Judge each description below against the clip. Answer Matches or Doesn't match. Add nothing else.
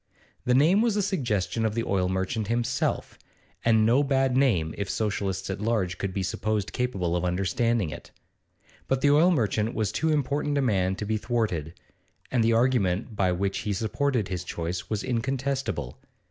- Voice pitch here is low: Matches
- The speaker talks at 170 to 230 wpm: Matches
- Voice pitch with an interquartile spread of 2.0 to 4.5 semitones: Doesn't match